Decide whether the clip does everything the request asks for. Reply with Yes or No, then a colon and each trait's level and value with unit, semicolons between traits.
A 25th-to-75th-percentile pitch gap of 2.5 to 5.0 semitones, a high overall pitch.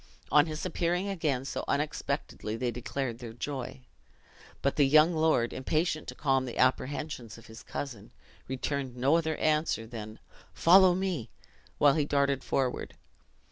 No: average, 4.1 semitones; medium, 140 Hz